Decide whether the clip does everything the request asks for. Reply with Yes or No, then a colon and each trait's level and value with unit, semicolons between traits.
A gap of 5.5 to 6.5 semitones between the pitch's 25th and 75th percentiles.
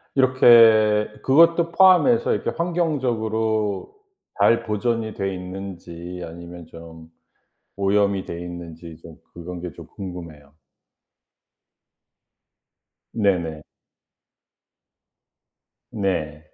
No: average, 5.1 semitones